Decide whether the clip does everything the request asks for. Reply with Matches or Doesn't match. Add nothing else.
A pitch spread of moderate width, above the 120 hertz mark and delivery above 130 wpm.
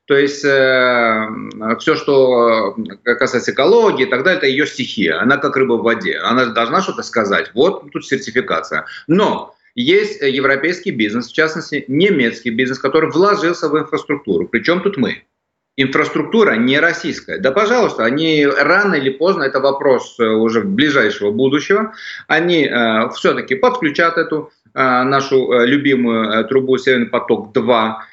Matches